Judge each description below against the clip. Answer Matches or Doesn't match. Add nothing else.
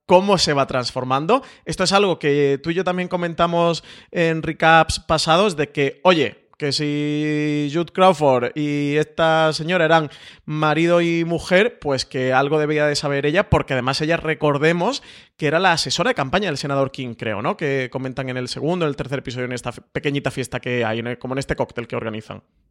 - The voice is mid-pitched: Matches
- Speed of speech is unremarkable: Doesn't match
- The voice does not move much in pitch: Doesn't match